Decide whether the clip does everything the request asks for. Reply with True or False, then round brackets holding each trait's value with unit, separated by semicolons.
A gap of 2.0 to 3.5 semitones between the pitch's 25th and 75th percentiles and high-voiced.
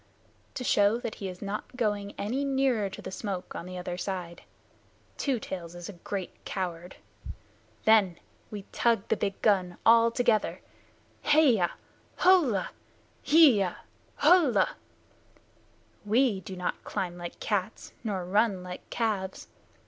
False (4.1 semitones; 205 Hz)